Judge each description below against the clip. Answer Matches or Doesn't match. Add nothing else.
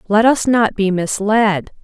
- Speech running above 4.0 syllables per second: Doesn't match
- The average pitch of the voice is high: Matches